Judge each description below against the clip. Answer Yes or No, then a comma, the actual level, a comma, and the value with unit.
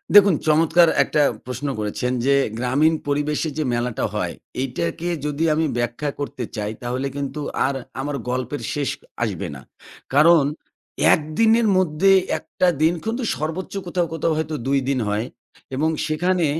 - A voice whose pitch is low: No, medium, 150 Hz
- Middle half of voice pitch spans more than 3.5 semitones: Yes, average, 4.2 semitones